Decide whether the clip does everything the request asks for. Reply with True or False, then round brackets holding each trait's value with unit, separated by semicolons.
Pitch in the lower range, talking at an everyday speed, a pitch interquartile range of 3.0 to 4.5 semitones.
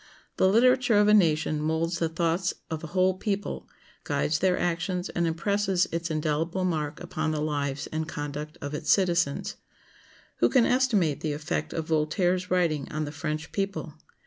False (165 Hz; 170 wpm; 3.4 semitones)